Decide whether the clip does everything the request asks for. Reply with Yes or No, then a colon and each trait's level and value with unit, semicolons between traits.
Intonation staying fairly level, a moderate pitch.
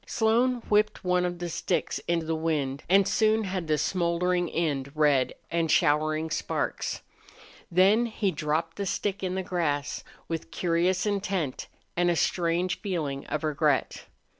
No: average, 3.4 semitones; medium, 170 Hz